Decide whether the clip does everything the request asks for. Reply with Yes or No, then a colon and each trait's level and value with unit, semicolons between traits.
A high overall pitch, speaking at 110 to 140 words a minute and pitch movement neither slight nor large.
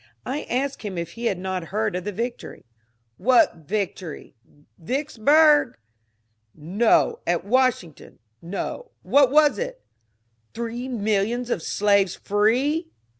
No: high, 220 Hz; slow, 135 wpm; wide, 6.1 semitones